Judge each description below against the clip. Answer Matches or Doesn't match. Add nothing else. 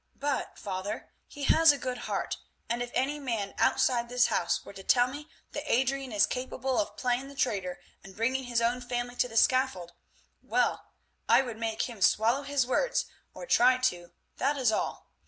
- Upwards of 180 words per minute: Matches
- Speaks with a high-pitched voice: Matches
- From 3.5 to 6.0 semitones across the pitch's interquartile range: Doesn't match